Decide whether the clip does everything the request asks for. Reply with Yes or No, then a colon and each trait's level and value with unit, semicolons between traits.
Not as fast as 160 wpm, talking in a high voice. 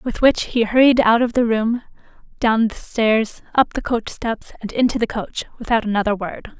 No: average, 190 wpm; high, 230 Hz